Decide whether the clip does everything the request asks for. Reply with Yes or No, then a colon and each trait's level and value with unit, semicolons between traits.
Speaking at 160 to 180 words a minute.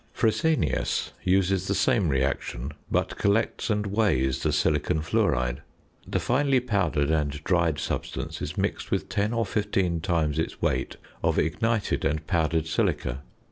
No: average, 140 wpm